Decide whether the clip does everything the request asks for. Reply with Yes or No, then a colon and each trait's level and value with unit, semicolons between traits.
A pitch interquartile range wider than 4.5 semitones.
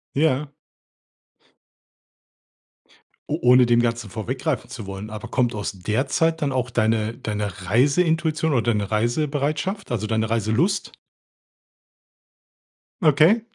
Yes: wide, 5.6 semitones